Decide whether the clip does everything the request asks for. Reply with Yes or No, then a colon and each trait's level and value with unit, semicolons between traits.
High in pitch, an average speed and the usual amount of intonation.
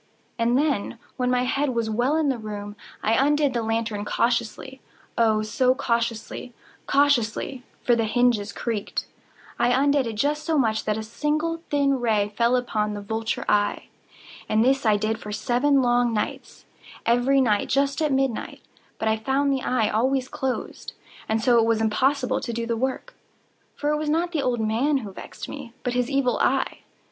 Yes: high, 245 Hz; average, 170 wpm; average, 3.7 semitones